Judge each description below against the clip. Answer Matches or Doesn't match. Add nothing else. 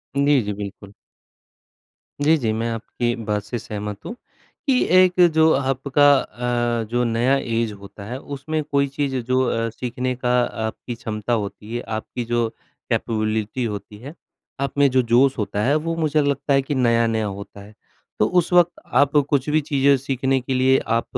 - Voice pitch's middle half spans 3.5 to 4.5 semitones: Matches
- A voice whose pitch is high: Doesn't match